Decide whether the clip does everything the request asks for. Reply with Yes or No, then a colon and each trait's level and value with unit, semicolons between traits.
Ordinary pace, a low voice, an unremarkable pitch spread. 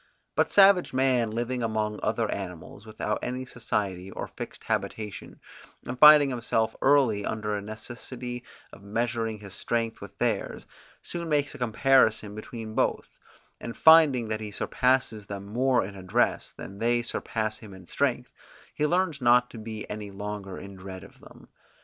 Yes: average, 160 wpm; low, 110 Hz; average, 3.4 semitones